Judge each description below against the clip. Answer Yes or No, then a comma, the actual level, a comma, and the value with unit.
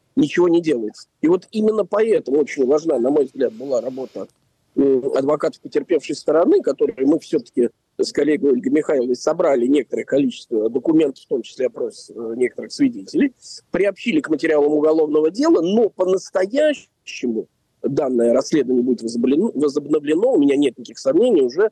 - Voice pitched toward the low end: No, high, 215 Hz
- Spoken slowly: No, average, 140 wpm